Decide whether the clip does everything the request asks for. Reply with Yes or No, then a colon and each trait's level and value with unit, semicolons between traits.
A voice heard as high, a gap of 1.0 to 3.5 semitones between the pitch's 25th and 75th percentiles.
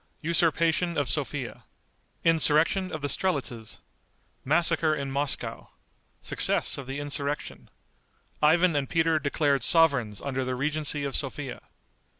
No: medium, 145 Hz; average, 2.8 semitones